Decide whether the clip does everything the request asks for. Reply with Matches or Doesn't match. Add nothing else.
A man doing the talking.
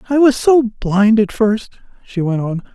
Matches